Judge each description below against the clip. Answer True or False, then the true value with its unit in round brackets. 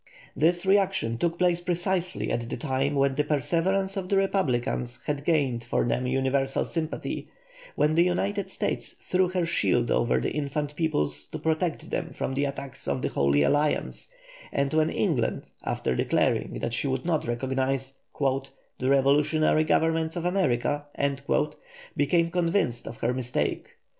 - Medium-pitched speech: True (145 Hz)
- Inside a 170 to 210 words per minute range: False (155 wpm)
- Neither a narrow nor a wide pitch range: True (4.6 semitones)